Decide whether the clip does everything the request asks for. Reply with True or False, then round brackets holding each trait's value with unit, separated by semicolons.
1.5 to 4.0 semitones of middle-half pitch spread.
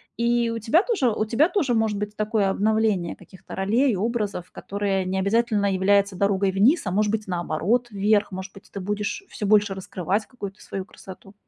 True (2.8 semitones)